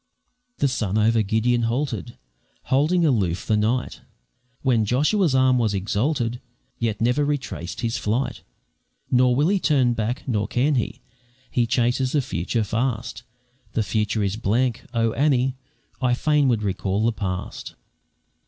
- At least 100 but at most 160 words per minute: Yes, average, 145 wpm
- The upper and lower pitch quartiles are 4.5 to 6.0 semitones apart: No, average, 3.4 semitones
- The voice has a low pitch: Yes, low, 120 Hz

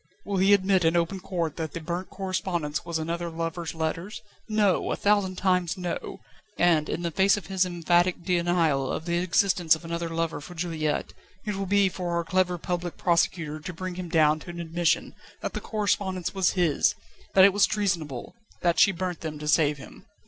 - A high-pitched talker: No, medium, 175 Hz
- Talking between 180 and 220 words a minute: Yes, average, 195 wpm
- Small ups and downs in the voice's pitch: Yes, narrow, 2.3 semitones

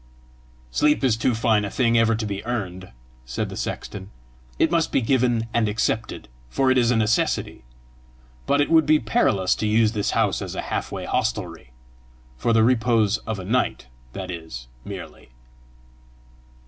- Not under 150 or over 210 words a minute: Yes, average, 170 wpm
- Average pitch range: Yes, average, 3.5 semitones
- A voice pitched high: No, low, 110 Hz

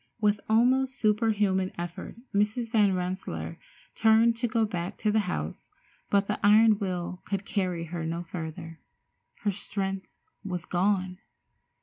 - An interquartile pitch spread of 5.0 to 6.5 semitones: No, average, 3.2 semitones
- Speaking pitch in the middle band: No, high, 200 Hz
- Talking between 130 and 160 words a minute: Yes, slow, 135 wpm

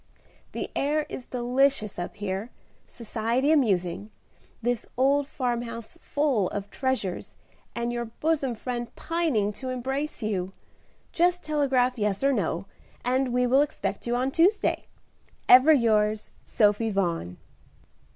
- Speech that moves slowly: Yes, slow, 125 wpm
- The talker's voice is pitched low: No, high, 245 Hz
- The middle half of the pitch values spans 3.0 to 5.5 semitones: Yes, average, 4.5 semitones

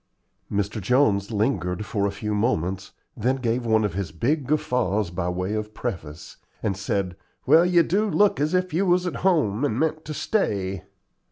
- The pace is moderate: Yes, average, 180 wpm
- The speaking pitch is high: No, low, 110 Hz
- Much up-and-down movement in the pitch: Yes, wide, 7.6 semitones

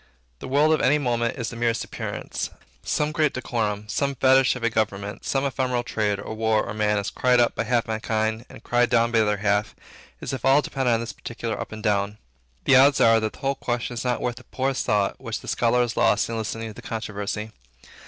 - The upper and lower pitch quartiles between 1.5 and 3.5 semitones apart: Yes, average, 2.8 semitones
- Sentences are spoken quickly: Yes, fast, 230 wpm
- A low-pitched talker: Yes, low, 115 Hz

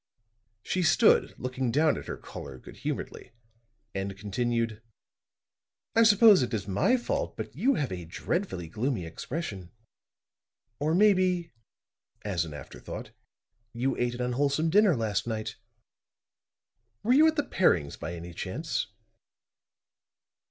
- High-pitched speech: No, low, 125 Hz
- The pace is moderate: No, slow, 130 wpm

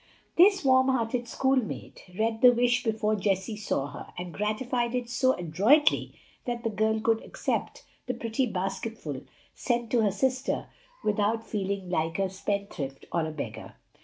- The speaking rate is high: No, average, 155 wpm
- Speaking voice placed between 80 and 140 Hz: No, high, 220 Hz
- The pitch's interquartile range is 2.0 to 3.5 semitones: No, average, 4.0 semitones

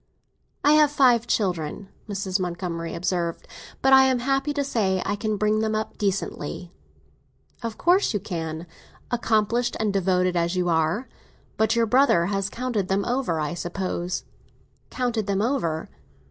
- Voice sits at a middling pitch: No, high, 205 Hz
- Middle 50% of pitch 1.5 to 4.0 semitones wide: No, average, 5.3 semitones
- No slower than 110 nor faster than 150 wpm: Yes, average, 145 wpm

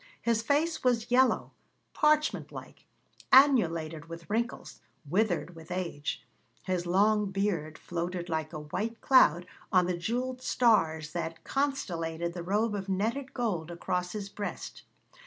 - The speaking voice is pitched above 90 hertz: Yes, high, 190 Hz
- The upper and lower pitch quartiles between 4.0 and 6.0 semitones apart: Yes, wide, 5.6 semitones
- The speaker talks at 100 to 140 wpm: Yes, slow, 135 wpm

